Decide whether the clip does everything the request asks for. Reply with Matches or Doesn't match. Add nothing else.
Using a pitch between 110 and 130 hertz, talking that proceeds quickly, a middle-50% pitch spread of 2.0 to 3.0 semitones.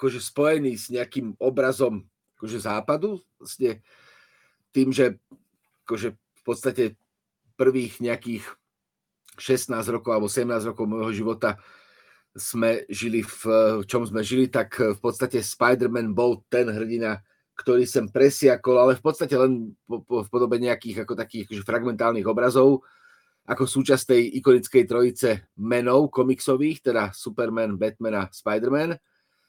Doesn't match